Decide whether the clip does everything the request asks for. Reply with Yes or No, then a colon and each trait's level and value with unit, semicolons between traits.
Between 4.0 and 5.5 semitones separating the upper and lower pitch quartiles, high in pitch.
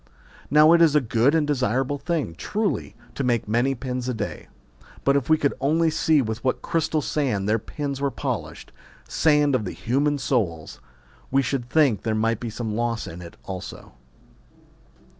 No: average, 4.6 semitones; low, 130 Hz